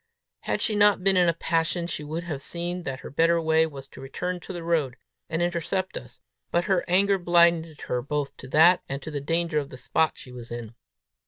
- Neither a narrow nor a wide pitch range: Yes, average, 3.4 semitones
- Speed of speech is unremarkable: No, fast, 225 wpm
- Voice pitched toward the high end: No, medium, 165 Hz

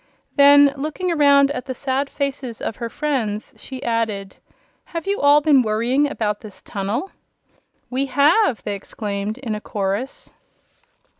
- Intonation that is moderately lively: Yes, average, 5.0 semitones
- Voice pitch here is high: Yes, very high, 260 Hz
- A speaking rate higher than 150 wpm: No, average, 145 wpm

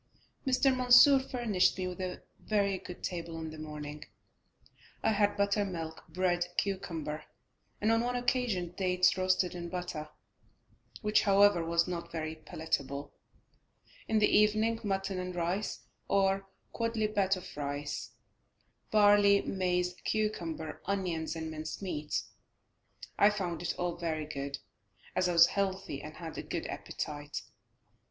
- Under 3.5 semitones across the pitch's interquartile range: No, average, 4.0 semitones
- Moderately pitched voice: Yes, medium, 180 Hz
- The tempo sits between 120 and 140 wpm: Yes, slow, 135 wpm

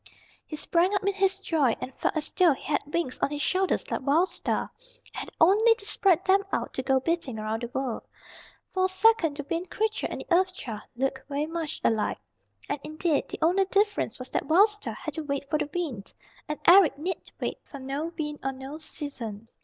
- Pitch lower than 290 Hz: No, very high, 315 Hz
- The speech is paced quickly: Yes, fast, 215 wpm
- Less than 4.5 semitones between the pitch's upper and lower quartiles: No, wide, 5.6 semitones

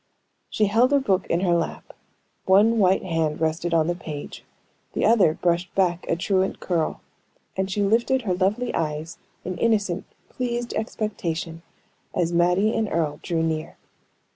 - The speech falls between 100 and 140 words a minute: No, average, 155 wpm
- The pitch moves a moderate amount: Yes, average, 4.2 semitones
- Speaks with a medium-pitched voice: Yes, medium, 180 Hz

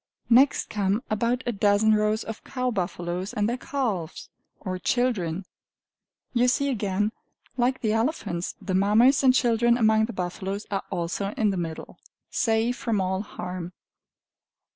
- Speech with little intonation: No, average, 4.1 semitones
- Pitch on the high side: Yes, high, 215 Hz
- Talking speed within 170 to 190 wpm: No, average, 145 wpm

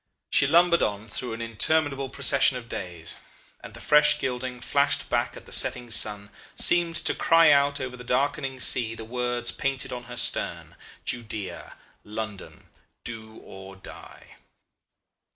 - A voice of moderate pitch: No, low, 125 Hz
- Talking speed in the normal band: Yes, average, 150 wpm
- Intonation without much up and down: No, average, 4.1 semitones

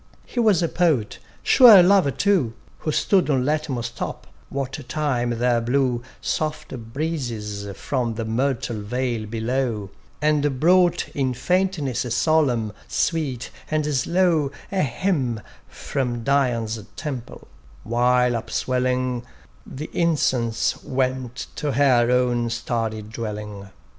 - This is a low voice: Yes, low, 130 Hz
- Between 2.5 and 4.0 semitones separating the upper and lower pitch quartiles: No, average, 4.5 semitones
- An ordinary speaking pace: No, slow, 120 wpm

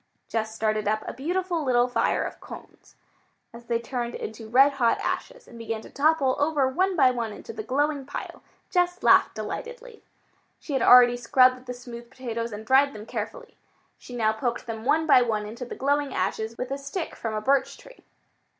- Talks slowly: No, average, 195 wpm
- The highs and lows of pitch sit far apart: No, average, 3.9 semitones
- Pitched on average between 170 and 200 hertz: No, very high, 255 Hz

